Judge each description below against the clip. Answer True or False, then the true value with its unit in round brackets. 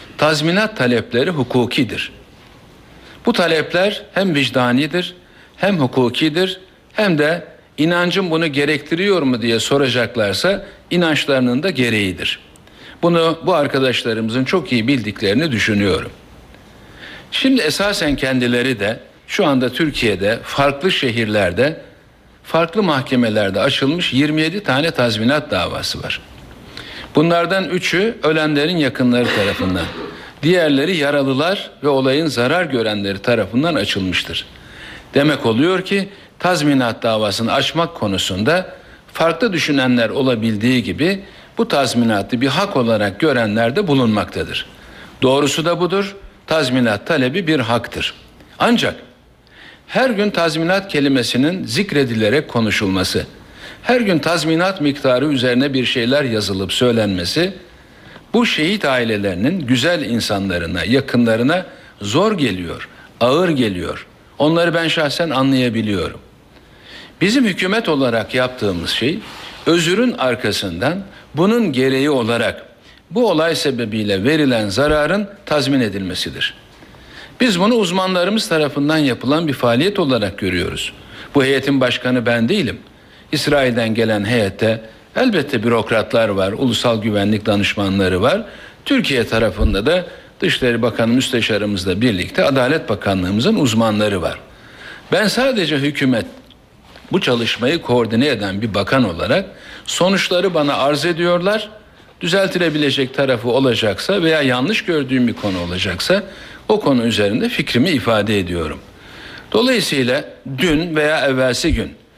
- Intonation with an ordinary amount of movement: False (6.5 semitones)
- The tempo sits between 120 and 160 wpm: False (105 wpm)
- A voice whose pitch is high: False (135 Hz)